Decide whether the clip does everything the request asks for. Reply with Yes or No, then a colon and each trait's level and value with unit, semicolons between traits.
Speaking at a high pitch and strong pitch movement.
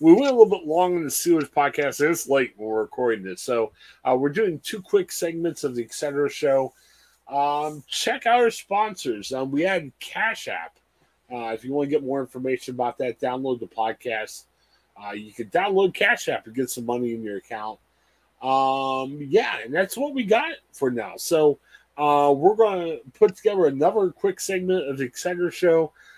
No: medium, 145 Hz; wide, 7.0 semitones